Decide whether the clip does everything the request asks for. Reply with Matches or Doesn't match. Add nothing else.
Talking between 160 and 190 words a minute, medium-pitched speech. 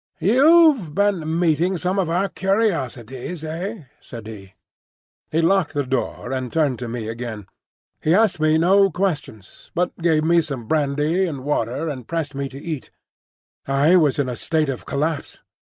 Matches